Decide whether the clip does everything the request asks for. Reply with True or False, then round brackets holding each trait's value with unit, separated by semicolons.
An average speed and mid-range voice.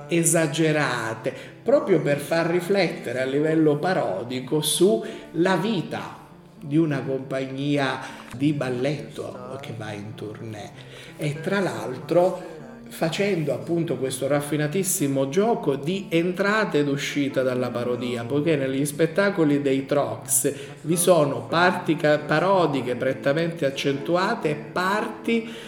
False (110 wpm; 150 Hz)